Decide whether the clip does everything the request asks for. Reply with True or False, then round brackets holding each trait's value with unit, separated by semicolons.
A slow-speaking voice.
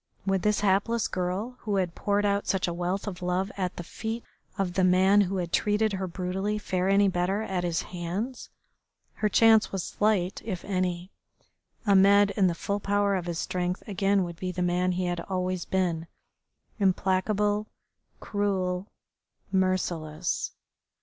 False (160 wpm)